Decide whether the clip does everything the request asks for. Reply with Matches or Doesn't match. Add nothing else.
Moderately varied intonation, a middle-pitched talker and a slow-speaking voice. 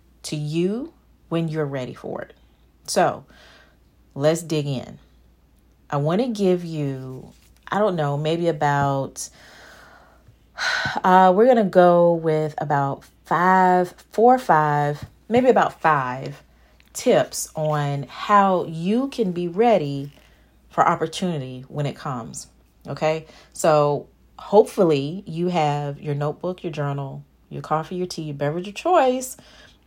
Matches